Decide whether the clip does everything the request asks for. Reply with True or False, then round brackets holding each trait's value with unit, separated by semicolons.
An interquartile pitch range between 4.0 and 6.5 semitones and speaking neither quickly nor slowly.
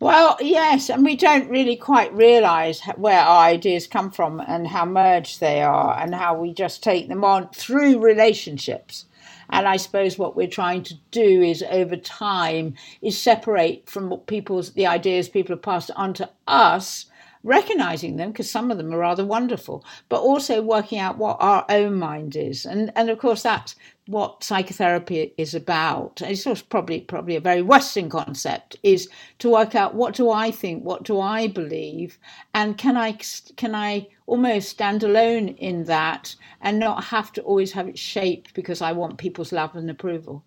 True (4.4 semitones; 180 wpm)